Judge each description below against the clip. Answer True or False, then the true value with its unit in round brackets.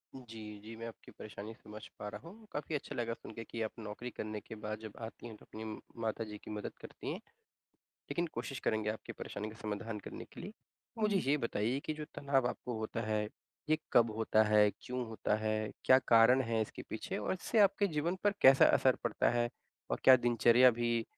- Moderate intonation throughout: True (3.2 semitones)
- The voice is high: False (115 Hz)